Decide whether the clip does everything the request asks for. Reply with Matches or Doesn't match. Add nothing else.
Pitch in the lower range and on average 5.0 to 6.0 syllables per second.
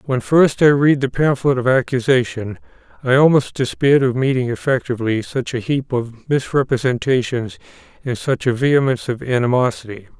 Matches